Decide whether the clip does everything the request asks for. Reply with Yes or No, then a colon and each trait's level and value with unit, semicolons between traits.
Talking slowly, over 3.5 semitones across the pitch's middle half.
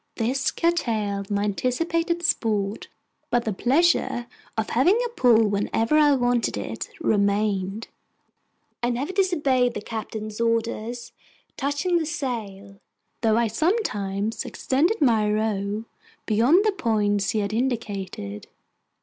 Yes: slow, 120 wpm; average, 5.2 semitones